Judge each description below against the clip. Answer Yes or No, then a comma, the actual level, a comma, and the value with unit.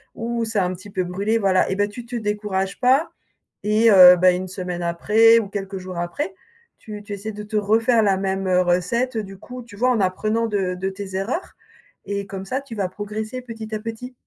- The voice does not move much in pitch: No, average, 3.1 semitones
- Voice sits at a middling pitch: No, high, 205 Hz